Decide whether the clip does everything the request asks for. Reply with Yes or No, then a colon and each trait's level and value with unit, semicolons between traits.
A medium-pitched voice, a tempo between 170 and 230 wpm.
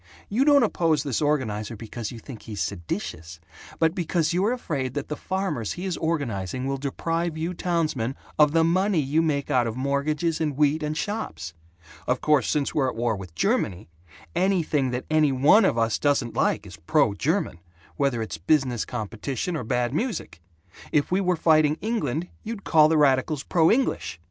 Yes: medium, 145 Hz; average, 180 wpm